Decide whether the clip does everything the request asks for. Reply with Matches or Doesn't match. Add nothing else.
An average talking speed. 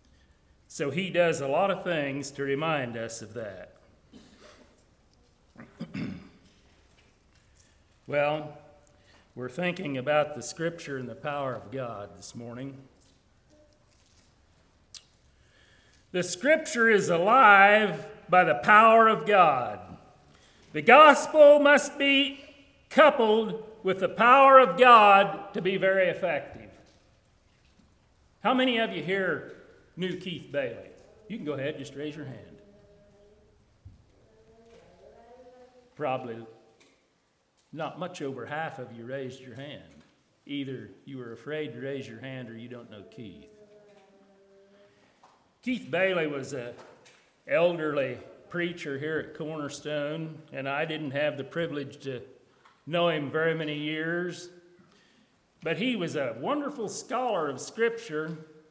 Doesn't match